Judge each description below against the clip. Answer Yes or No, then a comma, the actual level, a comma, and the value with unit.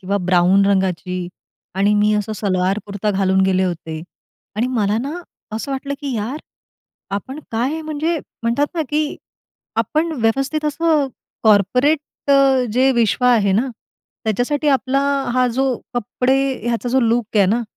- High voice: Yes, high, 230 Hz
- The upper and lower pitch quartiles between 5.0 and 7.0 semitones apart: Yes, average, 5.3 semitones